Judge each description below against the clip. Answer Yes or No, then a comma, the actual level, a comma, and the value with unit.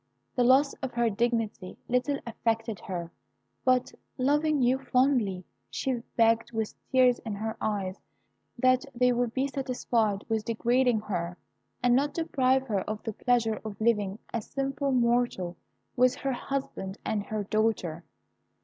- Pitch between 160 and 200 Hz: No, high, 235 Hz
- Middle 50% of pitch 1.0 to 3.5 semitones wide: Yes, average, 3.1 semitones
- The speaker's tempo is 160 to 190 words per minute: No, average, 150 wpm